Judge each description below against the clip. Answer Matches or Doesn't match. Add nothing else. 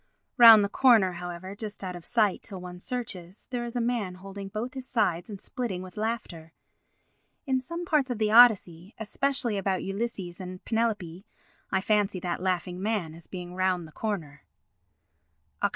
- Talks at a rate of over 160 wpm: Matches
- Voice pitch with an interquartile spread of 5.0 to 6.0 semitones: Doesn't match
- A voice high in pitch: Matches